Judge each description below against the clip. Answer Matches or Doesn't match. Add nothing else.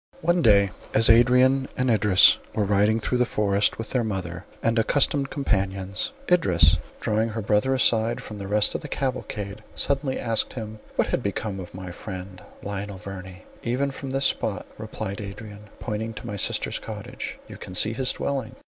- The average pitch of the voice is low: Matches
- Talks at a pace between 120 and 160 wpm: Doesn't match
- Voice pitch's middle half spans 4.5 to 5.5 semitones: Doesn't match